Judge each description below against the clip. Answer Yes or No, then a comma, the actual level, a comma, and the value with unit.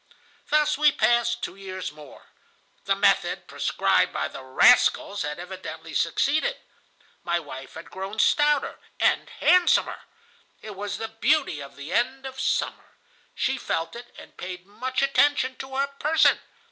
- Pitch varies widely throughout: Yes, wide, 7.2 semitones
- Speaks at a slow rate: No, average, 145 wpm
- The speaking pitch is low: No, high, 235 Hz